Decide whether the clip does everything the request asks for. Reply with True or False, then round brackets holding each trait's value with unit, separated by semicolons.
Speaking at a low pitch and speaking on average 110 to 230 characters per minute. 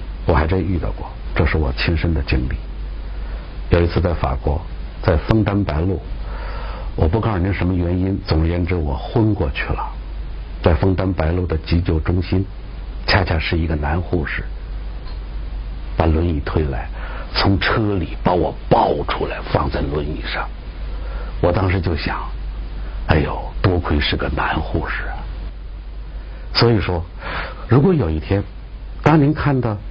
True (85 Hz; 215 characters per minute)